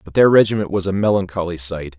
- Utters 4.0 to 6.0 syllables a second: No, 6.4 syllables/s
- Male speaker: Yes, male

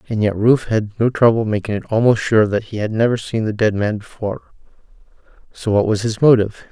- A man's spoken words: Yes, male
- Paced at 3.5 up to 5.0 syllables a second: No, 6.0 syllables/s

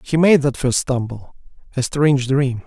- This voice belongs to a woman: No, male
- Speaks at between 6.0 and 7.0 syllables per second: No, 4.6 syllables/s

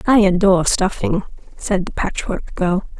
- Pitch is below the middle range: No, high, 190 Hz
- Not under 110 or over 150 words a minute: Yes, average, 140 wpm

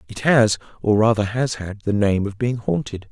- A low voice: Yes, low, 110 Hz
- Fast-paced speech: Yes, fast, 210 wpm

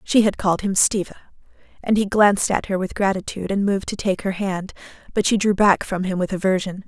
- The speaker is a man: No, female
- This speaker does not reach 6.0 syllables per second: No, 6.2 syllables/s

